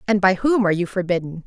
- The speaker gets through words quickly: Yes, fast, 245 wpm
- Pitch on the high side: Yes, high, 195 Hz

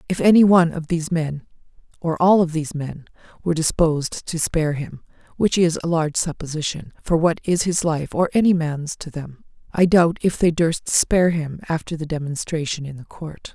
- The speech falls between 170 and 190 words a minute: Yes, average, 185 wpm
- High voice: No, medium, 160 Hz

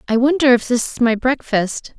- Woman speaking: Yes, female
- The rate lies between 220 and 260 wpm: No, fast, 210 wpm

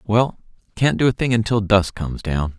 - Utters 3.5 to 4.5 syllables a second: No, 5.2 syllables/s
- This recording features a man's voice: Yes, male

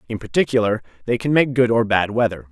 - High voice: No, low, 115 Hz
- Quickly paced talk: Yes, fast, 215 wpm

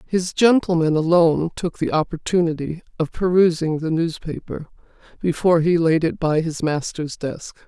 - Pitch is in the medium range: Yes, medium, 165 Hz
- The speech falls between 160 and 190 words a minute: No, average, 140 wpm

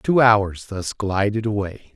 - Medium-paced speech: Yes, average, 155 wpm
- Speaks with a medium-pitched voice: No, low, 105 Hz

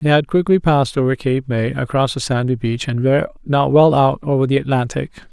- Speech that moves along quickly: Yes, fast, 215 wpm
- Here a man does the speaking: Yes, male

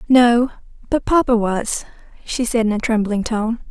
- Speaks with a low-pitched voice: No, high, 230 Hz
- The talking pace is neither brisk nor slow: Yes, average, 160 wpm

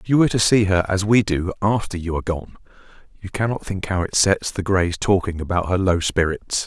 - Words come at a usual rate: No, fast, 235 wpm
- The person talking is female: No, male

